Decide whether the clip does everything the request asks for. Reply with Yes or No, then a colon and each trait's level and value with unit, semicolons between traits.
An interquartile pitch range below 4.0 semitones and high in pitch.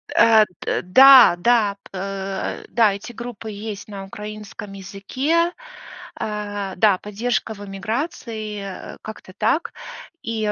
Yes: narrow, 2.6 semitones; high, 210 Hz